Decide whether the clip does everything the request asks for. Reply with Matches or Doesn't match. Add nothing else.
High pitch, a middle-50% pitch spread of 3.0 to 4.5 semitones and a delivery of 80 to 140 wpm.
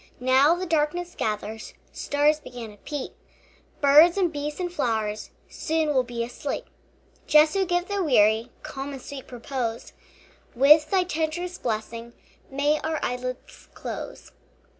Doesn't match